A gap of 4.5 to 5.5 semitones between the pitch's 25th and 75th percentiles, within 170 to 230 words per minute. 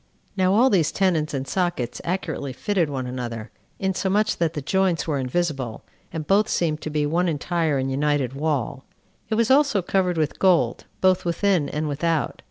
Yes: average, 4.9 semitones; average, 175 wpm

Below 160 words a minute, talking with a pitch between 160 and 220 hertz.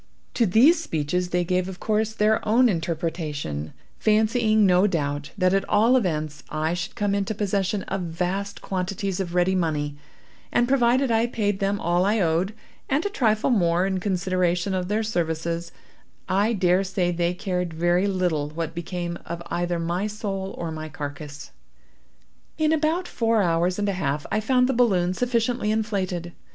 No: average, 165 wpm; medium, 185 Hz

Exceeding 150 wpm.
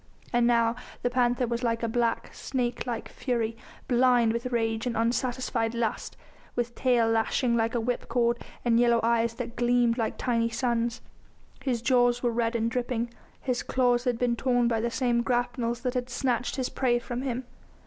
Yes: average, 180 wpm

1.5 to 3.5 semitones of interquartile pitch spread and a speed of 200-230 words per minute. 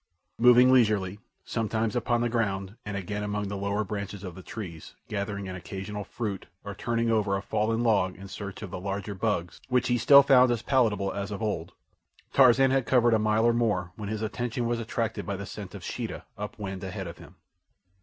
Yes: average, 2.9 semitones; fast, 205 wpm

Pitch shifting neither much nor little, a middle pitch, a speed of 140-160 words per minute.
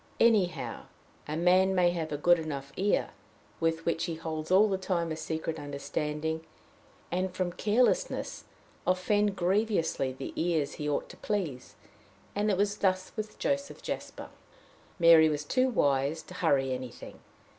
Yes: average, 3.8 semitones; medium, 170 Hz; average, 150 wpm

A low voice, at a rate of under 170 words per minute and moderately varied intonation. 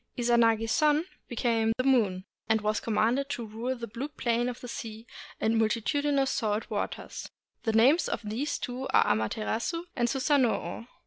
No: high, 235 Hz; average, 155 wpm; average, 3.0 semitones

